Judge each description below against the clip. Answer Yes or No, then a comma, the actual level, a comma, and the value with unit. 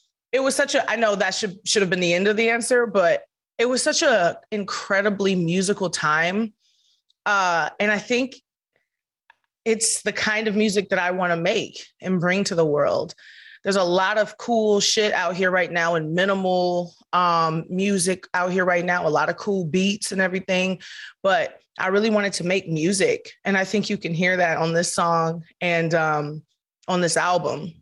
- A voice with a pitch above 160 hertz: Yes, high, 190 Hz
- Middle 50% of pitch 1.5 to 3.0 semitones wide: No, average, 3.4 semitones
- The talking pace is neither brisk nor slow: No, fast, 195 wpm